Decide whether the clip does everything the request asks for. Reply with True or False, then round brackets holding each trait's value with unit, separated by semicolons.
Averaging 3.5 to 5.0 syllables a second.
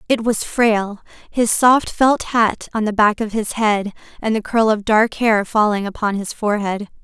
True (4.6 syllables/s)